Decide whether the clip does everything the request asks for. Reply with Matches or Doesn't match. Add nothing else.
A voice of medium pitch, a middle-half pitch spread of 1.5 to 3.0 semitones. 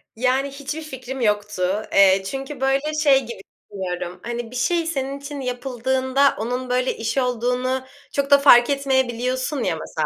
Doesn't match